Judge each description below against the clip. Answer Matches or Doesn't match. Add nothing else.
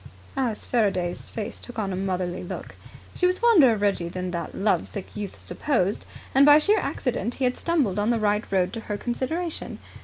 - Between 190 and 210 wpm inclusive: Matches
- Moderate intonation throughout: Doesn't match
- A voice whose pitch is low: Doesn't match